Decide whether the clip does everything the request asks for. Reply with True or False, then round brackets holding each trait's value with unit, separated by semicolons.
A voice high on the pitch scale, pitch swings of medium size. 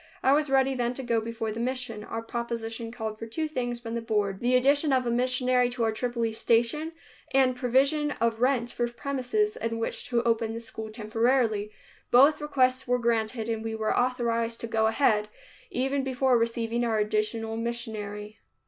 False (235 Hz; 2.2 semitones)